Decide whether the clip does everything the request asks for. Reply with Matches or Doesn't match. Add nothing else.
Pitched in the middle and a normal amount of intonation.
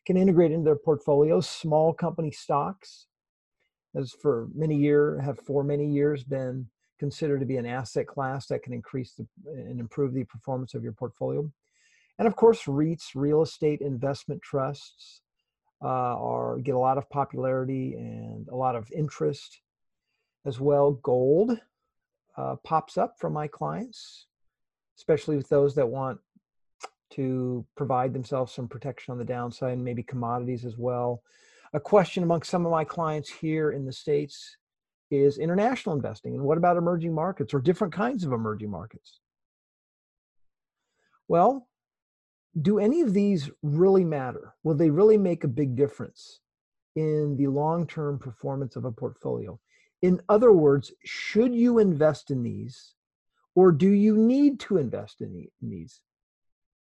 Matches